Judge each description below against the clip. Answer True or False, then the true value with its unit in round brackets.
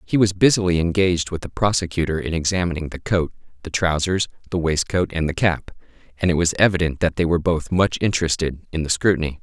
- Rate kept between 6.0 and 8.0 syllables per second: True (6.1 syllables/s)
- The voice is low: True (85 Hz)